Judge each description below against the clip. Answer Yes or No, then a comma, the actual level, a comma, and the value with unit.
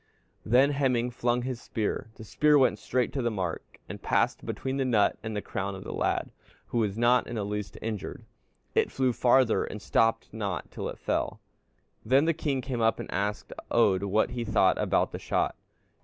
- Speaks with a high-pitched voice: No, low, 115 Hz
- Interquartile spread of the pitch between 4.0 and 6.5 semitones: No, average, 3.5 semitones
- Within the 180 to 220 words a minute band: Yes, average, 200 wpm